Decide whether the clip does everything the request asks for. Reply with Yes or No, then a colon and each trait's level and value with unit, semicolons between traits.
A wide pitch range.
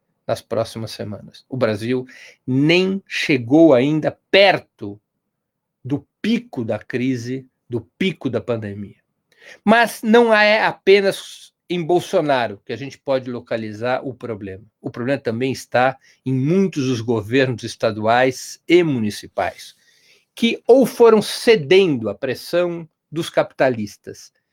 Yes: wide, 7.6 semitones